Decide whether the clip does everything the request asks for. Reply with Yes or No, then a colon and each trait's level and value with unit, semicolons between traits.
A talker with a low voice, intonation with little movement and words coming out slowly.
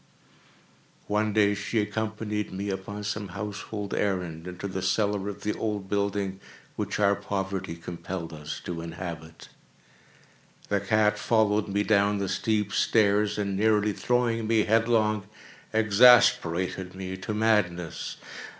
Yes: low, 100 Hz; narrow, 2.1 semitones; slow, 130 wpm